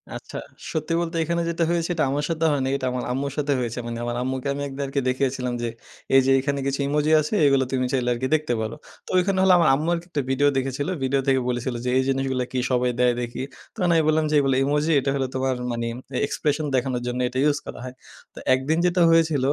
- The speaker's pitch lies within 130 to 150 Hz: Yes, low, 135 Hz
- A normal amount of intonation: Yes, average, 3.2 semitones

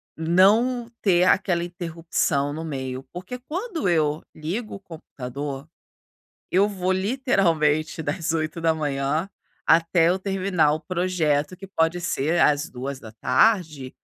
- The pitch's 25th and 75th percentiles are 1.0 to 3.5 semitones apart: No, average, 3.9 semitones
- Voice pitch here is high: No, medium, 165 Hz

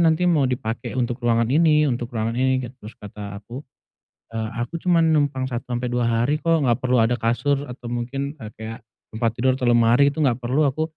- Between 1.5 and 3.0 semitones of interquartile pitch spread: No, average, 3.4 semitones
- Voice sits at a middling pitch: No, low, 125 Hz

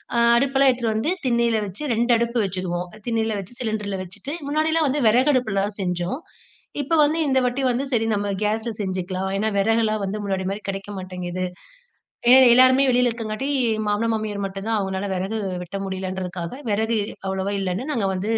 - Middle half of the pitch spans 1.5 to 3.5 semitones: No, average, 4.1 semitones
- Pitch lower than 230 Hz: Yes, high, 215 Hz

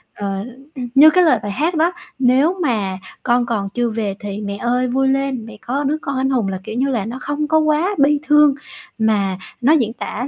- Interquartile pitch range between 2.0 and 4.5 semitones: No, average, 5.0 semitones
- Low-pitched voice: No, very high, 250 Hz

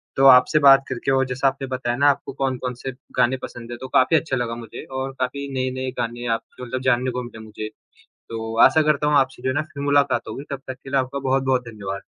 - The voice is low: Yes, low, 130 Hz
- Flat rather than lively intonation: Yes, narrow, 2.0 semitones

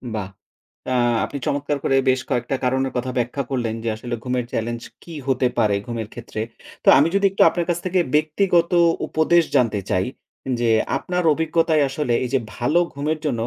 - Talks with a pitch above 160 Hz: No, low, 135 Hz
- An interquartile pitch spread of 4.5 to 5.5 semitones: Yes, average, 4.8 semitones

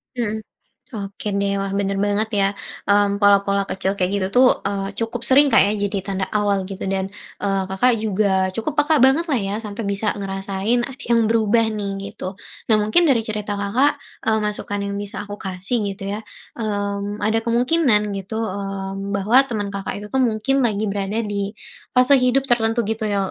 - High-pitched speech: Yes, high, 205 Hz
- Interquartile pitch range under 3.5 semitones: Yes, narrow, 2.4 semitones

